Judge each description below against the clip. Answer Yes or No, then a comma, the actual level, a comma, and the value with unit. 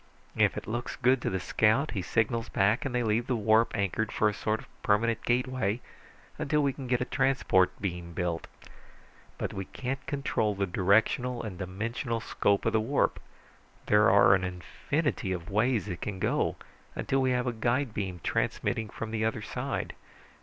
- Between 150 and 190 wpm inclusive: Yes, average, 180 wpm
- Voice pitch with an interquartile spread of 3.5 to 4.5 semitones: Yes, average, 4.1 semitones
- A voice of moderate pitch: No, low, 110 Hz